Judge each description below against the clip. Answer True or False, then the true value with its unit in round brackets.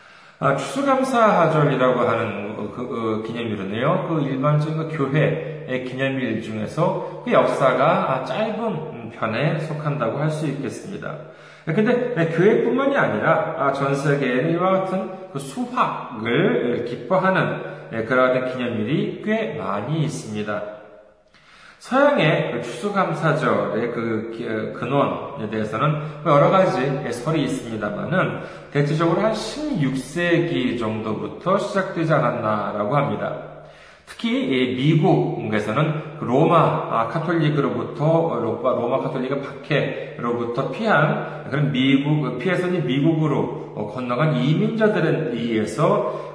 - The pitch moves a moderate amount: False (6.4 semitones)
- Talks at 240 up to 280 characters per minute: True (265 characters per minute)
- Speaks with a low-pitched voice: False (150 Hz)